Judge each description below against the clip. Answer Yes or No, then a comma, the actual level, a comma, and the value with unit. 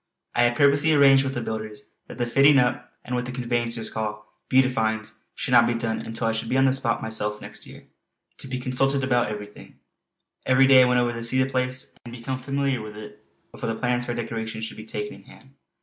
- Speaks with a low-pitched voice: Yes, low, 120 Hz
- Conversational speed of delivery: No, fast, 225 wpm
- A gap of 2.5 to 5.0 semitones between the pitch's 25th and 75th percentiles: Yes, average, 2.8 semitones